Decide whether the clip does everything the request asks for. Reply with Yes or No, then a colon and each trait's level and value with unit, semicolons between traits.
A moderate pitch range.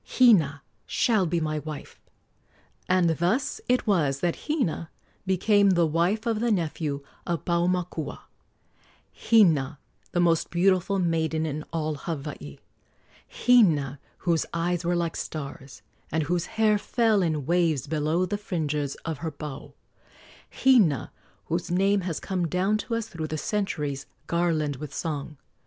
Yes: average, 3.9 semitones